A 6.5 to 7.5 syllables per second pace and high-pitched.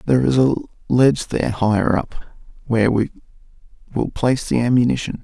No: 6.9 syllables/s; low, 125 Hz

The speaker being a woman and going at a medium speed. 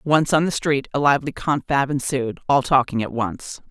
Yes: female; average, 195 wpm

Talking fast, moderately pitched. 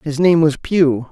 Yes: fast, 215 wpm; medium, 155 Hz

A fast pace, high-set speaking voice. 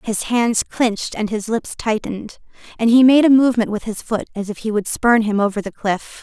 Yes: fast, 230 wpm; high, 220 Hz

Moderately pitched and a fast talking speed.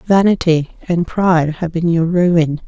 No: medium, 170 Hz; average, 155 wpm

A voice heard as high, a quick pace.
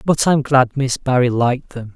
No: low, 130 Hz; fast, 215 wpm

